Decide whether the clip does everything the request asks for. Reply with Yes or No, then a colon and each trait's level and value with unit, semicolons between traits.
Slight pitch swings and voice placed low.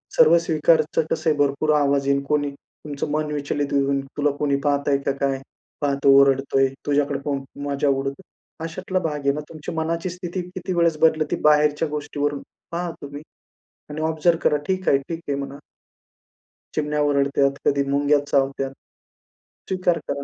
No: narrow, 2.2 semitones; medium, 145 Hz